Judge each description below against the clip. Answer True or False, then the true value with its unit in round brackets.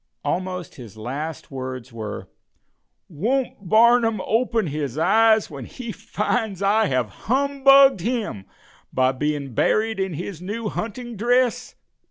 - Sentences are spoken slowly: True (125 wpm)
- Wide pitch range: True (8.3 semitones)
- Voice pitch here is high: True (200 Hz)